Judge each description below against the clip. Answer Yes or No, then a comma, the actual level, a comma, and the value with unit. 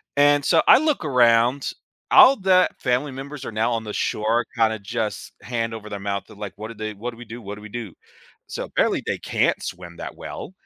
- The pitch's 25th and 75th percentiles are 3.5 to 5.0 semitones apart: Yes, average, 4.0 semitones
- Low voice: Yes, low, 115 Hz